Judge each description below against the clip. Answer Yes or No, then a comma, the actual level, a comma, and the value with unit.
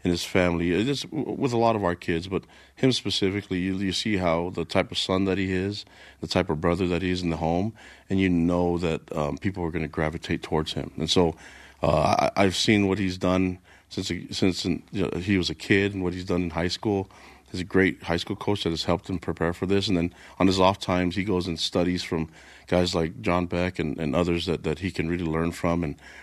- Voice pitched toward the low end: Yes, very low, 90 Hz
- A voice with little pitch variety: Yes, narrow, 2.0 semitones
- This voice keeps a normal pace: No, fast, 250 wpm